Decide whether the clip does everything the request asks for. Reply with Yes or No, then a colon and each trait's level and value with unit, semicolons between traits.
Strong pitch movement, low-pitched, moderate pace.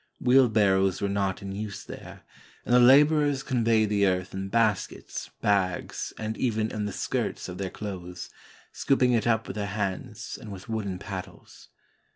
No: average, 3.1 semitones; low, 105 Hz; average, 170 wpm